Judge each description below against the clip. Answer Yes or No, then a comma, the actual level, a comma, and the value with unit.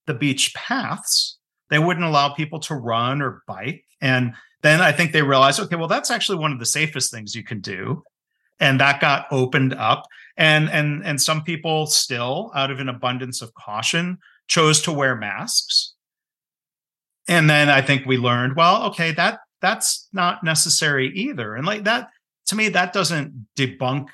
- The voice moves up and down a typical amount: Yes, average, 3.9 semitones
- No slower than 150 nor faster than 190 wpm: Yes, average, 175 wpm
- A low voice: No, medium, 150 Hz